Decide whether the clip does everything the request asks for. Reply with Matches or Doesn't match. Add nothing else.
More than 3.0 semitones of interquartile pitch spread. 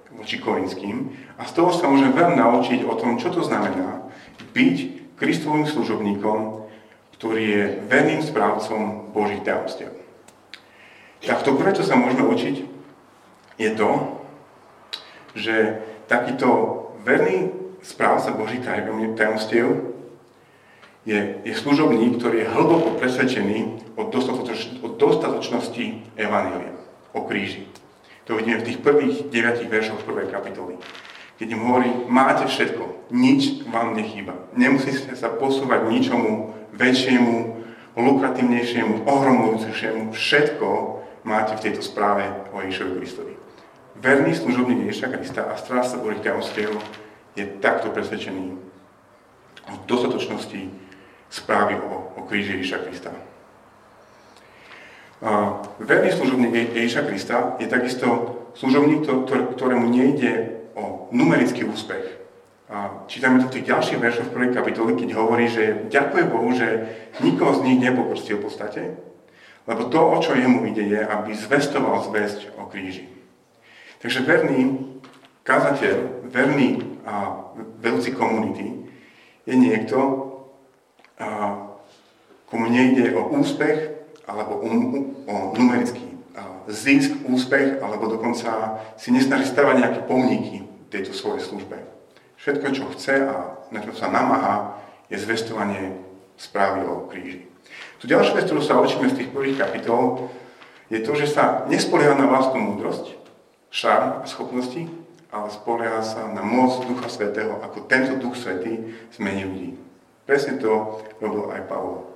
Matches